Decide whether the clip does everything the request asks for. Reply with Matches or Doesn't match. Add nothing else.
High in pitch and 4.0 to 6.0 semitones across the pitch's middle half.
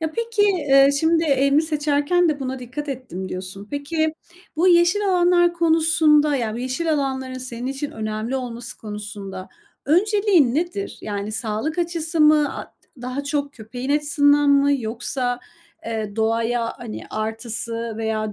Matches